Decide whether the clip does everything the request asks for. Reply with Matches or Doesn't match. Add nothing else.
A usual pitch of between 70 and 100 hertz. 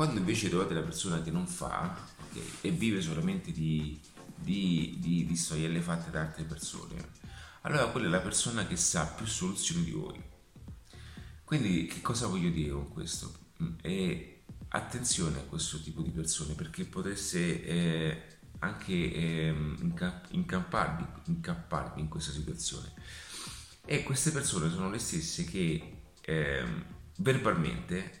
Matches